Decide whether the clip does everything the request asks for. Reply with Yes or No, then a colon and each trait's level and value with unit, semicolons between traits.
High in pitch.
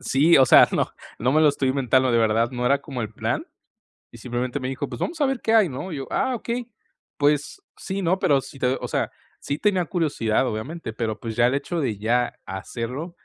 No: low, 135 Hz